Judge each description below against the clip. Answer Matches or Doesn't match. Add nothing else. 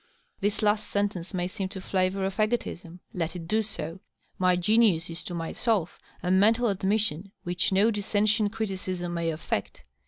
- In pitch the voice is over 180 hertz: Matches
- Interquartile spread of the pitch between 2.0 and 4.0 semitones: Matches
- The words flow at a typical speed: Matches